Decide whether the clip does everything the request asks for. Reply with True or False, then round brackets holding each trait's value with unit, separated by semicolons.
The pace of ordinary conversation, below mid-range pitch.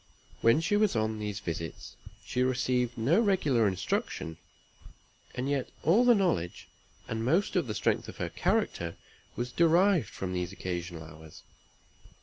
True (145 wpm; 120 Hz)